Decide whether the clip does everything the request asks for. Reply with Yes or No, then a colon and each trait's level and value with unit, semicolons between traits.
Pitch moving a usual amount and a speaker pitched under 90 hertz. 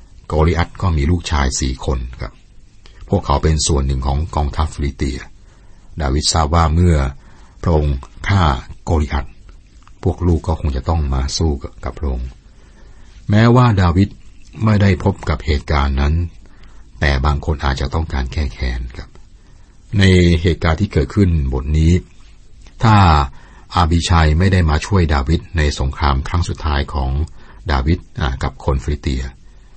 Yes: average, 4.3 semitones; very low, 80 Hz